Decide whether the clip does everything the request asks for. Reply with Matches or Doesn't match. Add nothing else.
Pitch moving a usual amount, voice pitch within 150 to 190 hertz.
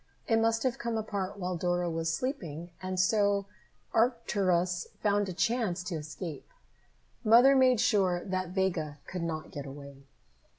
Matches